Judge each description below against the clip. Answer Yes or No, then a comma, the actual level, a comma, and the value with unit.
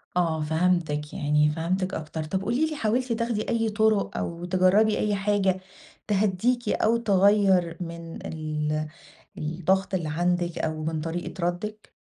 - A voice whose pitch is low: No, medium, 180 Hz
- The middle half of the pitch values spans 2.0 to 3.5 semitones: No, average, 4.4 semitones